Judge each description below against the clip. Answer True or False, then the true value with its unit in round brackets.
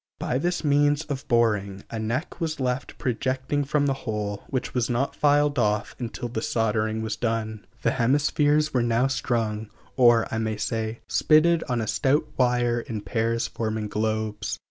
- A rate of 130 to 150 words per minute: False (165 wpm)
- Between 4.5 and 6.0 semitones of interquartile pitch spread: False (4.0 semitones)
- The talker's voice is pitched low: True (120 Hz)